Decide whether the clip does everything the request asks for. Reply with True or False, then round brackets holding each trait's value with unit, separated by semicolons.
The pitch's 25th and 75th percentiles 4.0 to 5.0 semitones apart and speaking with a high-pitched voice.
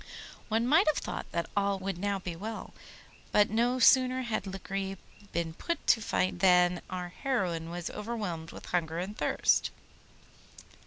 True (4.3 semitones; 195 Hz)